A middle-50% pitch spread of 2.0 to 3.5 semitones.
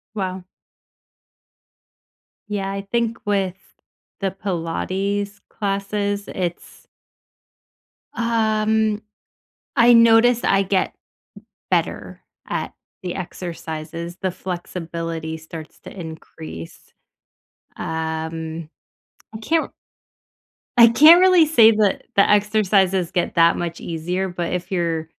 No: average, 4.2 semitones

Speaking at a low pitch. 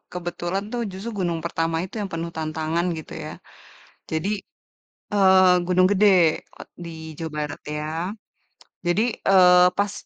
No: medium, 175 Hz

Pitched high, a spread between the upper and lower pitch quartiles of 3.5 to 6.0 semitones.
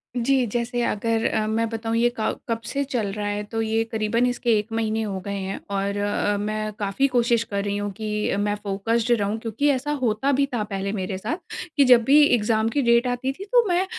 No: high, 225 Hz; average, 2.9 semitones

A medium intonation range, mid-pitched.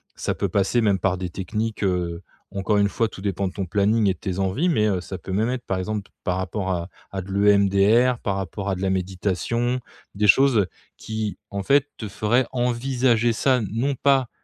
No: average, 3.7 semitones; low, 100 Hz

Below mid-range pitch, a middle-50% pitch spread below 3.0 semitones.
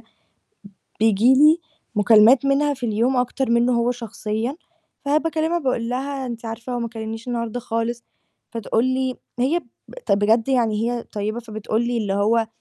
No: high, 235 Hz; narrow, 2.6 semitones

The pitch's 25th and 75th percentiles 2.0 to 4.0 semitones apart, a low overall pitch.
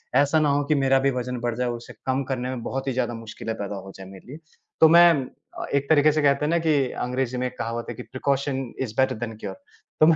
Yes: average, 2.8 semitones; low, 130 Hz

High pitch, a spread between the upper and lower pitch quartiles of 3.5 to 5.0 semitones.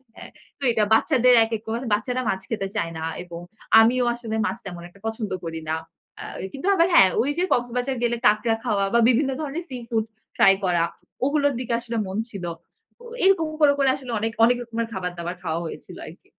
Yes: high, 230 Hz; average, 4.5 semitones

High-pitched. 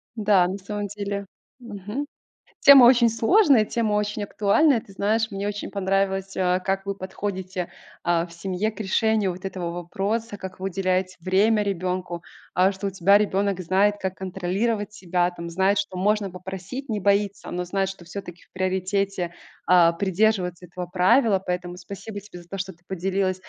Yes: high, 195 Hz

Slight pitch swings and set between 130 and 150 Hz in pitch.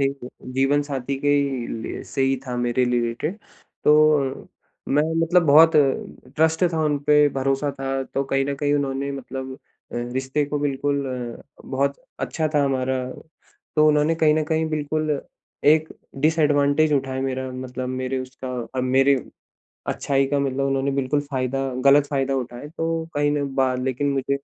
Yes: narrow, 2.0 semitones; medium, 140 Hz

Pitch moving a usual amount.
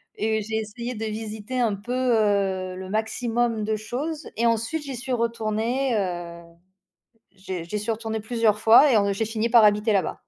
No: narrow, 2.2 semitones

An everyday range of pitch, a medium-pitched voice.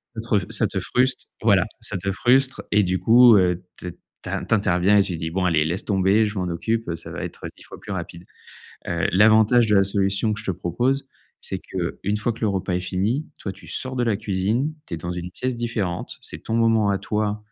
No: average, 3.7 semitones; low, 100 Hz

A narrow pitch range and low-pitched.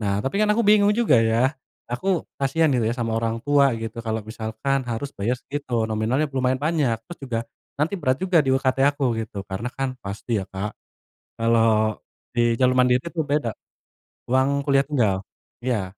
No: average, 4.0 semitones; low, 125 Hz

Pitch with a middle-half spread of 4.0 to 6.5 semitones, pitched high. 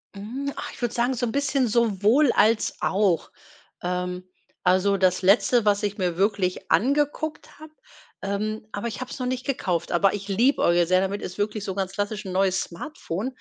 Yes: average, 4.5 semitones; high, 205 Hz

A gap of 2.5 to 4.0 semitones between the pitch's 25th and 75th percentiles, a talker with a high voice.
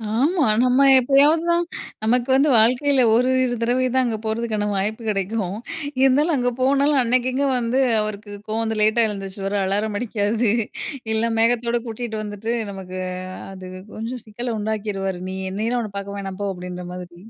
Yes: average, 3.6 semitones; high, 225 Hz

